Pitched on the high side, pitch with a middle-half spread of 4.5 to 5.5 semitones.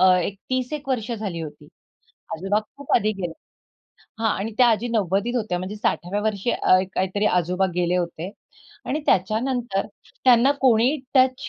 Yes: high, 215 Hz; average, 4.8 semitones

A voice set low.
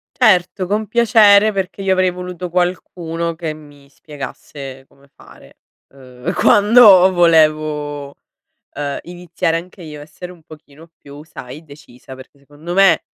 No: medium, 165 Hz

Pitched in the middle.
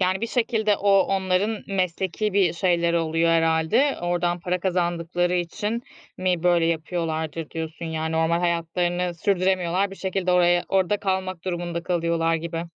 Yes: medium, 175 Hz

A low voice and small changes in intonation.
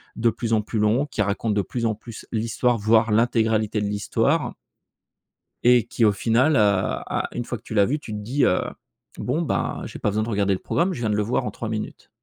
Yes: low, 110 Hz; narrow, 2.3 semitones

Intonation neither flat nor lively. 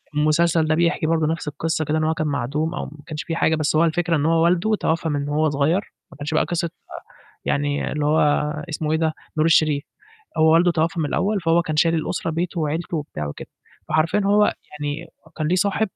No: narrow, 1.8 semitones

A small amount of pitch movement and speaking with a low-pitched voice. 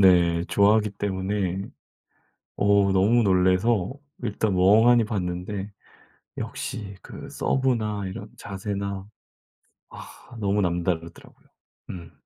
Yes: narrow, 2.2 semitones; low, 100 Hz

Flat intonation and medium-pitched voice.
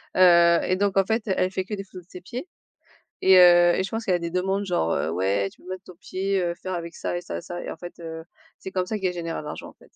Yes: narrow, 1.9 semitones; medium, 180 Hz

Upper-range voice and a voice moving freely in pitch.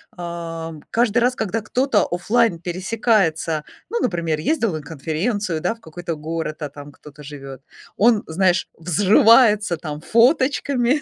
No: medium, 175 Hz; wide, 6.2 semitones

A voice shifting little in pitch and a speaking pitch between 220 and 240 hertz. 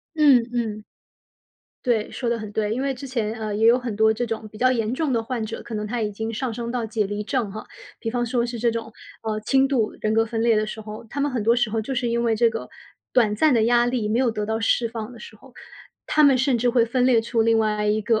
Yes: narrow, 2.2 semitones; high, 230 Hz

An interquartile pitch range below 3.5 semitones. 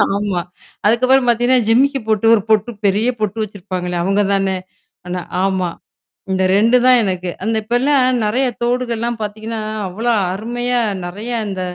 No: average, 3.8 semitones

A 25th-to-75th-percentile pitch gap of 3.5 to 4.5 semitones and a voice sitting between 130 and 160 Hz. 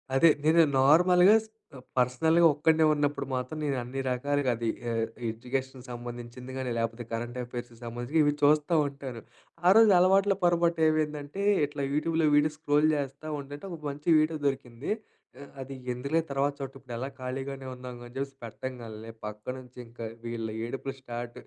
Yes: average, 4.0 semitones; low, 135 Hz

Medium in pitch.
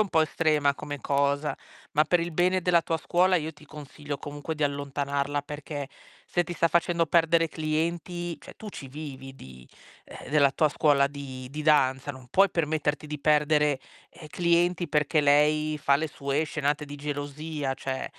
Yes: medium, 150 Hz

